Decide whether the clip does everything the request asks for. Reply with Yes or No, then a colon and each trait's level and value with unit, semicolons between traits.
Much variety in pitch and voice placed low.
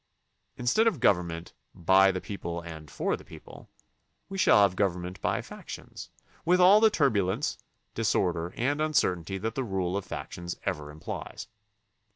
Yes: wide, 5.9 semitones; very low, 95 Hz